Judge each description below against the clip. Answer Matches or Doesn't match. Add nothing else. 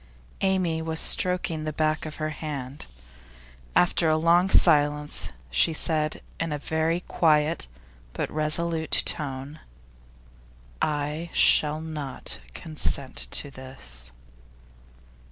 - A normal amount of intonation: Doesn't match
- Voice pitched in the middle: Matches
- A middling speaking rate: Doesn't match